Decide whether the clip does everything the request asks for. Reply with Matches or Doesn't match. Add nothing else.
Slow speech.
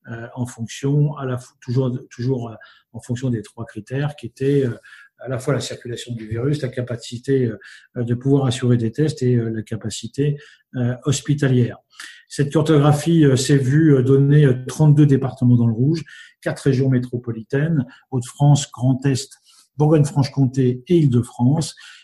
Matches